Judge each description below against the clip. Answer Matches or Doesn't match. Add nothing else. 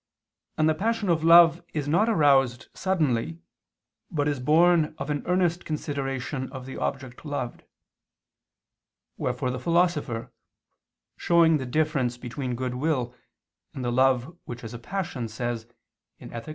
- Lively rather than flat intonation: Doesn't match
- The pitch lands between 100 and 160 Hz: Matches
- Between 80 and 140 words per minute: Matches